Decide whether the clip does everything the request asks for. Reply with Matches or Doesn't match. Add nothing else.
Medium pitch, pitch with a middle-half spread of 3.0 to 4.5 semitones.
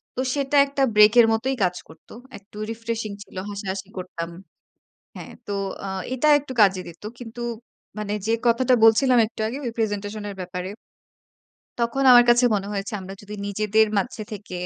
Doesn't match